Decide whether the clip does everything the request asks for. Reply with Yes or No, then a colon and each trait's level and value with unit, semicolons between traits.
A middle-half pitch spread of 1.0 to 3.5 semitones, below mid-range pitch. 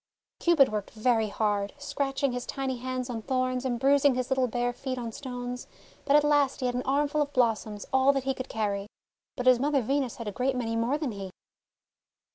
No: average, 2.8 semitones; very high, 255 Hz